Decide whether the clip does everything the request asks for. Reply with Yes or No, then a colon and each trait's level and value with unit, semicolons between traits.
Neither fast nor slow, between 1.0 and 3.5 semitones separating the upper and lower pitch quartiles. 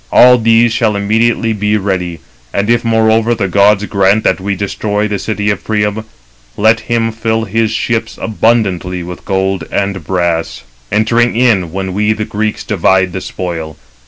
Yes: average, 165 wpm; average, 2.8 semitones